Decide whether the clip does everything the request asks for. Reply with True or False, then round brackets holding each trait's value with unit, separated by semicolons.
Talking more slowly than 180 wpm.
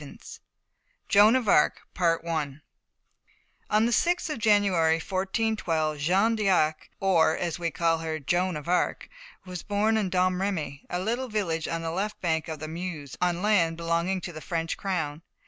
True (160 wpm)